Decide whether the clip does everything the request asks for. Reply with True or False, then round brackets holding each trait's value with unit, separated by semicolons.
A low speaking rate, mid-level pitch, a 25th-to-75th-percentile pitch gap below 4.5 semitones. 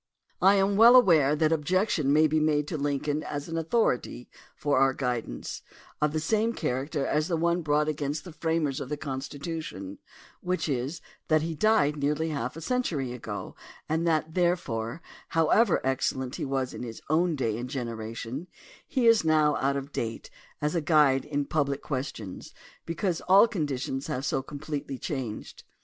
False (170 wpm; 150 Hz; 3.5 semitones)